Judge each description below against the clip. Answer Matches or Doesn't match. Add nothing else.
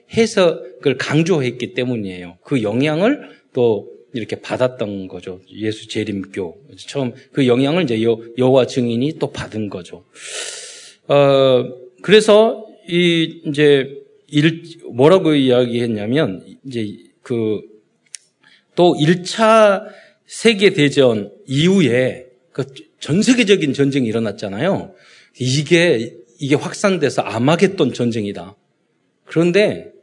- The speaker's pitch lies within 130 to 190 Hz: Matches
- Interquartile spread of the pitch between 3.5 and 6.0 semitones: Doesn't match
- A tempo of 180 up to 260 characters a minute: Matches